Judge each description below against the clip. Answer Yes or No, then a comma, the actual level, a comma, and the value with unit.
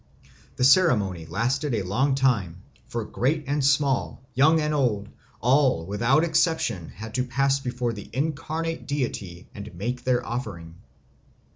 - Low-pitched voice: Yes, low, 125 Hz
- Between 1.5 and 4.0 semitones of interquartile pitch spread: No, average, 5.2 semitones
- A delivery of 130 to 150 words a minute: Yes, average, 140 wpm